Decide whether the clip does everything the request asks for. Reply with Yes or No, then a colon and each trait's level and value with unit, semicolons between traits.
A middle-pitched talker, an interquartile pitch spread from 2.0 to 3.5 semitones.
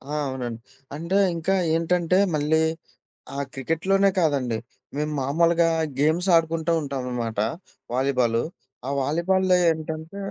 No: medium, 160 Hz; average, 4.1 semitones